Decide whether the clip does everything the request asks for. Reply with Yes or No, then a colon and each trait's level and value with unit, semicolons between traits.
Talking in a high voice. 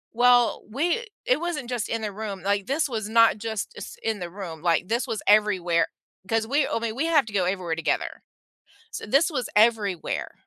Yes: high, 220 Hz